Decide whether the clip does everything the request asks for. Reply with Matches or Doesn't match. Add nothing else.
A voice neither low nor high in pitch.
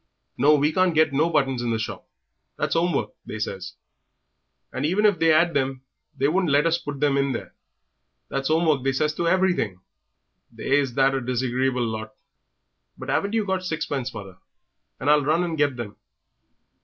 Matches